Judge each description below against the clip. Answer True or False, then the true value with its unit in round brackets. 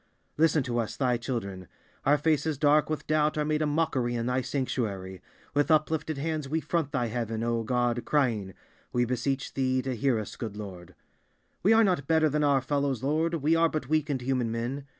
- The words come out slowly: False (190 wpm)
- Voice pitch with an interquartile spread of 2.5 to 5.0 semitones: True (4.3 semitones)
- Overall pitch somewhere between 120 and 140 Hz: True (135 Hz)